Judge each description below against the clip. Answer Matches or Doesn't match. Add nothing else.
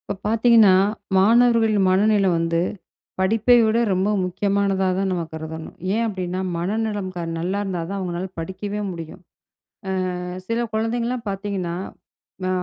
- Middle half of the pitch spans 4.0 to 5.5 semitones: Doesn't match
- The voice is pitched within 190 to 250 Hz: Matches